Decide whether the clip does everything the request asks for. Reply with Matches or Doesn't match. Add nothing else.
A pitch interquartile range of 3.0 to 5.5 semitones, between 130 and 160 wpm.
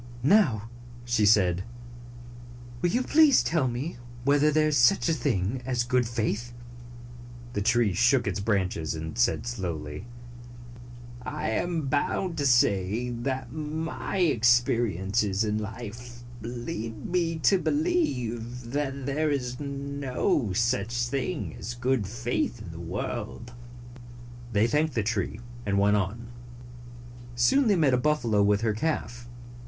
Matches